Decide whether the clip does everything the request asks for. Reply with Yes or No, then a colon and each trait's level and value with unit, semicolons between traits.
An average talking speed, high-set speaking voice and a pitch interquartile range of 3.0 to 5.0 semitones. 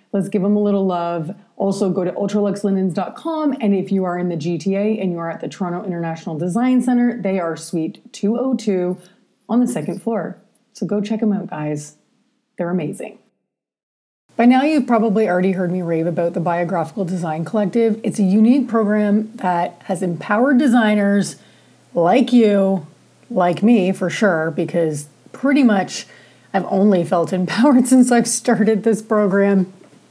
Yes: average, 165 wpm; high, 200 Hz; average, 4.1 semitones